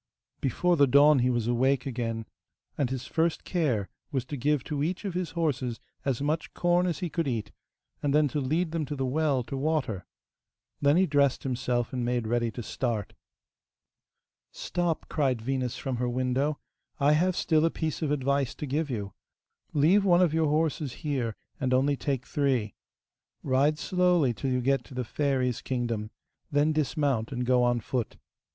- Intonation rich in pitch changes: No, average, 3.7 semitones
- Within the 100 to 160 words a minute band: No, average, 180 wpm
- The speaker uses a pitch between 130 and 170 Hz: Yes, medium, 140 Hz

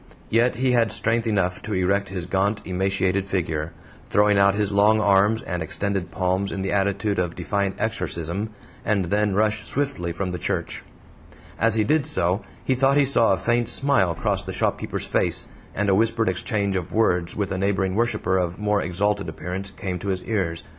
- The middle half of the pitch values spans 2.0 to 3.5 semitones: Yes, average, 2.8 semitones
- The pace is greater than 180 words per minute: Yes, average, 190 wpm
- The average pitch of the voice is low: Yes, low, 100 Hz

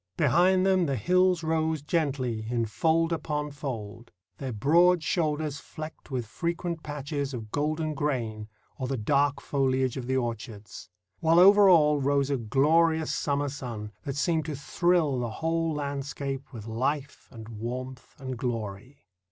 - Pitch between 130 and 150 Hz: Yes, medium, 140 Hz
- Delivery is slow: No, average, 150 wpm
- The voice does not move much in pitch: No, average, 4.3 semitones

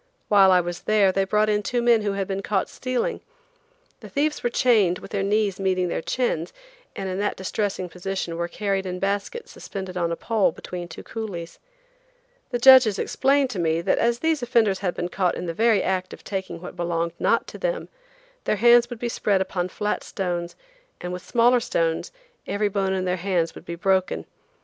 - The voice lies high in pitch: Yes, high, 195 Hz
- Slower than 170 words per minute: No, average, 200 wpm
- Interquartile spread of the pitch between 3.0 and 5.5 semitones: Yes, average, 3.7 semitones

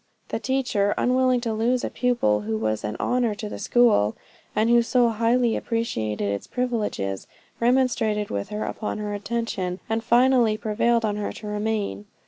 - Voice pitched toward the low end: No, high, 220 Hz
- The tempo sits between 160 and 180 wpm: Yes, average, 165 wpm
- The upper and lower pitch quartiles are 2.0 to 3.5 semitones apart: Yes, average, 2.8 semitones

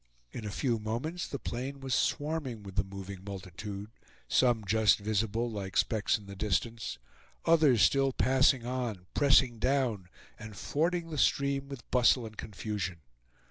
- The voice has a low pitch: Yes, low, 115 Hz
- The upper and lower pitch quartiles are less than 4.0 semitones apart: No, average, 4.9 semitones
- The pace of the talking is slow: No, average, 150 wpm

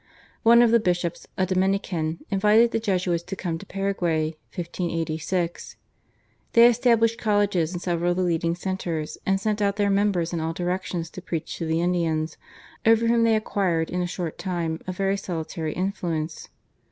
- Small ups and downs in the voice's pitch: No, average, 3.2 semitones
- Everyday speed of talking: Yes, average, 170 wpm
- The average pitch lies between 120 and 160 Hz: No, medium, 180 Hz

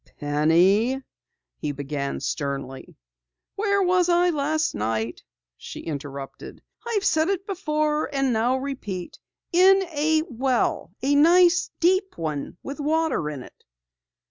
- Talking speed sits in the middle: No, slow, 120 wpm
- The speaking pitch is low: No, very high, 275 Hz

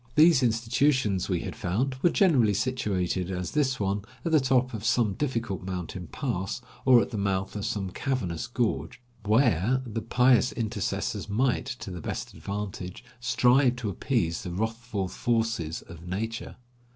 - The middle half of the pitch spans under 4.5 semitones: No, average, 4.8 semitones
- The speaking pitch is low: Yes, low, 110 Hz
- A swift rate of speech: No, average, 155 wpm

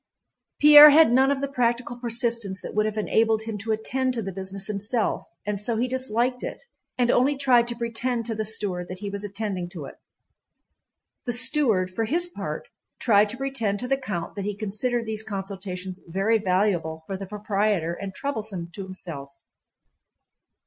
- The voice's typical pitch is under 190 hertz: No, high, 215 Hz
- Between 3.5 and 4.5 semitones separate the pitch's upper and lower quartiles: Yes, average, 3.8 semitones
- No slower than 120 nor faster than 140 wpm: No, average, 180 wpm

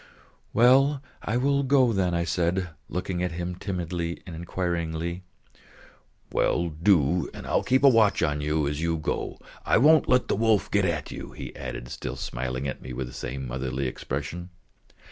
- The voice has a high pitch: No, very low, 85 Hz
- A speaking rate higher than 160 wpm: Yes, average, 170 wpm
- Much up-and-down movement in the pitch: Yes, wide, 5.8 semitones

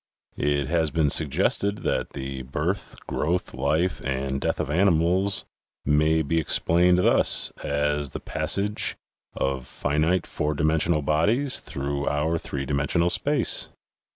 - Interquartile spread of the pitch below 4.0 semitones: Yes, average, 3.5 semitones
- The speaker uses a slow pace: Yes, slow, 125 wpm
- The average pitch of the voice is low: Yes, very low, 75 Hz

